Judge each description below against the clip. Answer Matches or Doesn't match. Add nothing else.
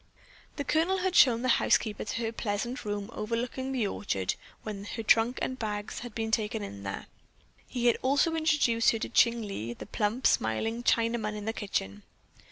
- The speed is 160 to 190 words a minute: Matches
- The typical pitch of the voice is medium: Doesn't match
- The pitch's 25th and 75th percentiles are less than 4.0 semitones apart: Matches